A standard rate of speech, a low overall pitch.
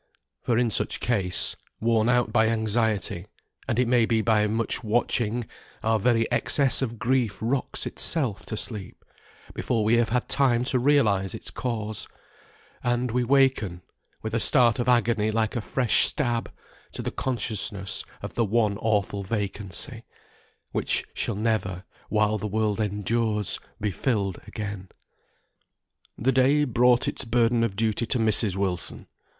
Yes: average, 150 wpm; low, 115 Hz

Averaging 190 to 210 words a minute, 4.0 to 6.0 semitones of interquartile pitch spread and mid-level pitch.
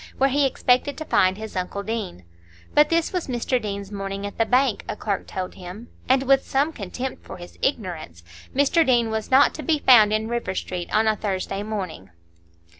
No: average, 195 wpm; average, 5.1 semitones; high, 220 Hz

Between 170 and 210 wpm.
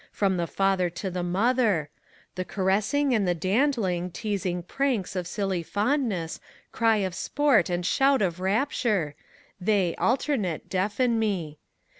No: slow, 135 wpm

